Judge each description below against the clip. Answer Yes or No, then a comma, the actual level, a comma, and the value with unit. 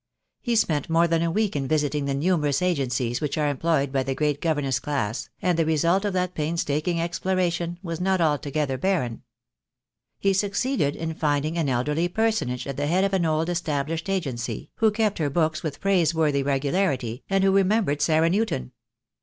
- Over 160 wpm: Yes, average, 180 wpm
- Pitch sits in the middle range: Yes, medium, 160 Hz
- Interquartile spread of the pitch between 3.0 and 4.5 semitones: Yes, average, 4.2 semitones